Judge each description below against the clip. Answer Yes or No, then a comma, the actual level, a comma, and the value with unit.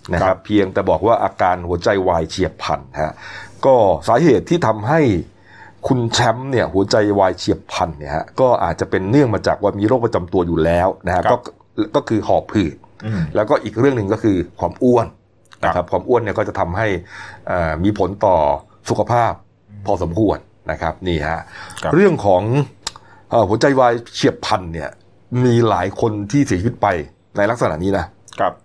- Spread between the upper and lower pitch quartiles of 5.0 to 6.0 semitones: No, average, 4.5 semitones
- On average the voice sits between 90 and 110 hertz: Yes, low, 100 Hz